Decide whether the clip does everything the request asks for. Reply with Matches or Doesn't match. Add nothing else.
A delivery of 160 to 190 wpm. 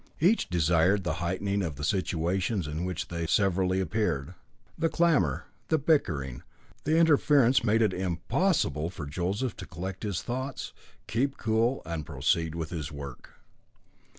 Doesn't match